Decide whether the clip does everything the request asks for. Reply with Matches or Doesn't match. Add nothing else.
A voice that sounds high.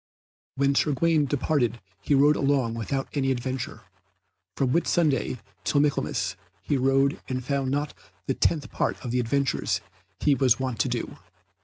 Doesn't match